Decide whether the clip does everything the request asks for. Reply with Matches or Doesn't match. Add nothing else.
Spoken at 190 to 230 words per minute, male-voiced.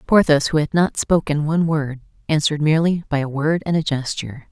Doesn't match